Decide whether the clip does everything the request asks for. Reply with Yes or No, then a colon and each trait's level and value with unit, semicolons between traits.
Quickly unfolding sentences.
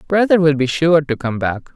Yes: fast, 240 wpm